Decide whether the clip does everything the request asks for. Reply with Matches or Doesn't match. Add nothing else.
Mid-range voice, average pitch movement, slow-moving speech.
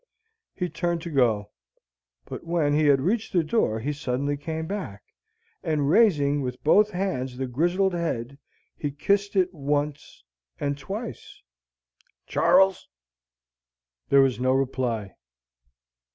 Matches